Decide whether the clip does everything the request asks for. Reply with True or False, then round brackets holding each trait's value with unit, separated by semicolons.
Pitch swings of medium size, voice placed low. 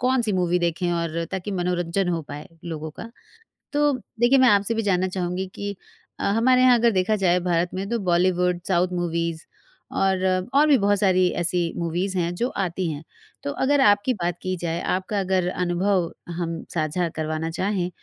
False (3.0 semitones; 180 Hz)